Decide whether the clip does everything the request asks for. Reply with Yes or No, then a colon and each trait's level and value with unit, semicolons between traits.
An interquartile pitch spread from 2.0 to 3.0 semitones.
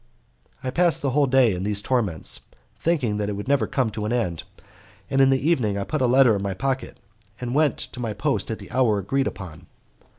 No: average, 4.6 semitones